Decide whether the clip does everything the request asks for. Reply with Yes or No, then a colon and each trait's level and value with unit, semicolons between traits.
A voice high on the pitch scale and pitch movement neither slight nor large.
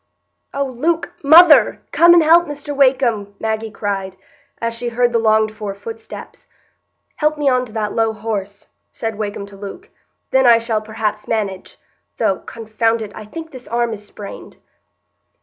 Yes: high, 225 Hz; average, 4.3 semitones